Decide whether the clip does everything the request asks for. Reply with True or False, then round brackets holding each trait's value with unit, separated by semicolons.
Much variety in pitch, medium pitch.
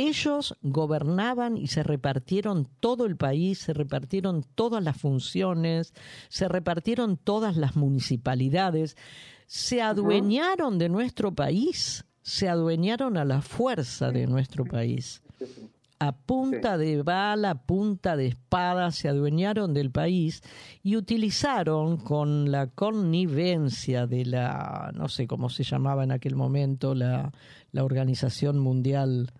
True (6.2 semitones; 155 Hz)